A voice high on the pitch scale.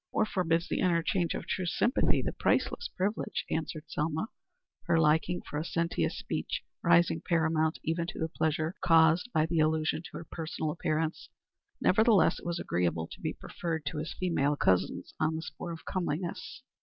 No: medium, 165 Hz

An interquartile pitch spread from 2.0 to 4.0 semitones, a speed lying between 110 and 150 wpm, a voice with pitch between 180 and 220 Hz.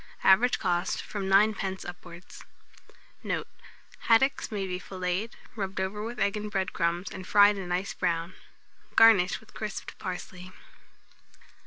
Yes: narrow, 2.5 semitones; slow, 135 wpm; high, 190 Hz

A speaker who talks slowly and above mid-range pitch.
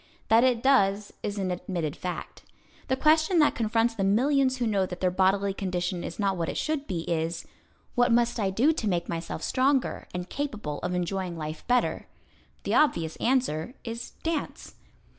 No: average, 180 wpm; high, 200 Hz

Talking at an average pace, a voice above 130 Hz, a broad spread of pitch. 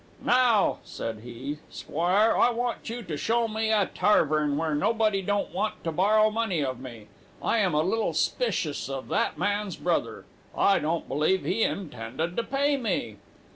Yes: average, 170 wpm; high, 190 Hz; wide, 6.7 semitones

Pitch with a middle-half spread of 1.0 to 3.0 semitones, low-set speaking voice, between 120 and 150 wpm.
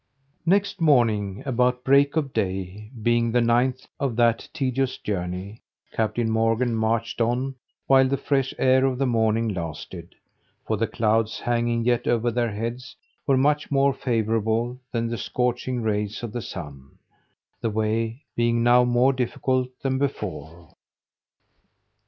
Yes: narrow, 2.6 semitones; low, 120 Hz; average, 140 wpm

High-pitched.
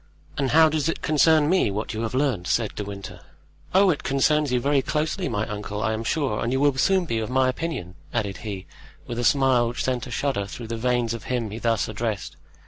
No: low, 125 Hz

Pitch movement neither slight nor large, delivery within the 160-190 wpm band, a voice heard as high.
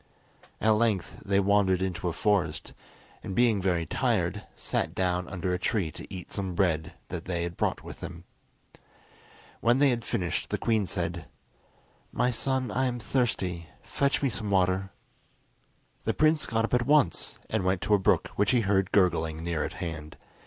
No: average, 4.3 semitones; average, 175 wpm; very low, 95 Hz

